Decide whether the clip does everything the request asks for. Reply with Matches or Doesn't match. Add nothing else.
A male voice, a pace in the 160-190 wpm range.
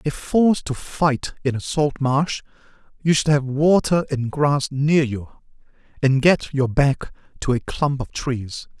Matches